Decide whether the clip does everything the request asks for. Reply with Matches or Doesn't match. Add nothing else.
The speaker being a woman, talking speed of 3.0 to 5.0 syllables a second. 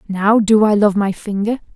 Matches